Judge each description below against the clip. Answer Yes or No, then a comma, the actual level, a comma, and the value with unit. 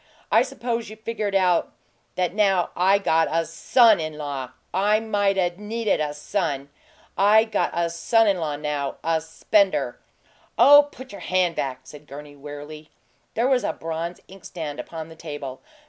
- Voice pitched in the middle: Yes, medium, 175 Hz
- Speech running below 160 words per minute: No, average, 170 wpm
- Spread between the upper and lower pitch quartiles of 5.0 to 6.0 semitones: Yes, wide, 5.5 semitones